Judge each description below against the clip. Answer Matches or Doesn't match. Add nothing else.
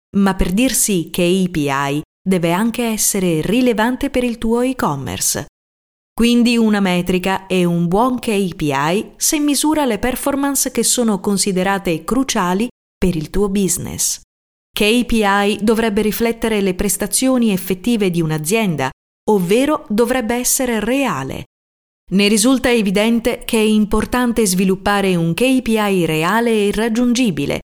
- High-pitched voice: Matches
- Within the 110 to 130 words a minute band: Matches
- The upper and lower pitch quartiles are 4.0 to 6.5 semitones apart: Matches